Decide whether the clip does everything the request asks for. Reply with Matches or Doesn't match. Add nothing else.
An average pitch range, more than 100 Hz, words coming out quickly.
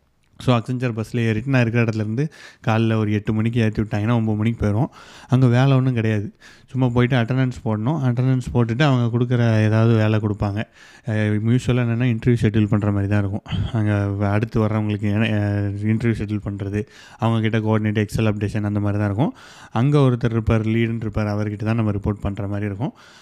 Doesn't match